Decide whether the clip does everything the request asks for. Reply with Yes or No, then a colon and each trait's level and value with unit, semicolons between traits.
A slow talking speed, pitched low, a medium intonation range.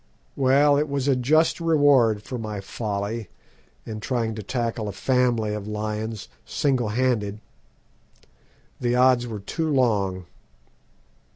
Yes: slow, 125 wpm; low, 115 Hz; average, 3.6 semitones